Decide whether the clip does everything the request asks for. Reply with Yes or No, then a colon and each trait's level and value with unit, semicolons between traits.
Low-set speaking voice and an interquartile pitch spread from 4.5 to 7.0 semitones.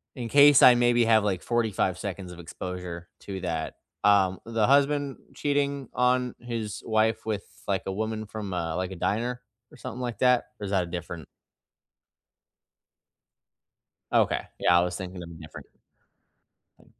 Yes: low, 105 Hz; average, 5.0 semitones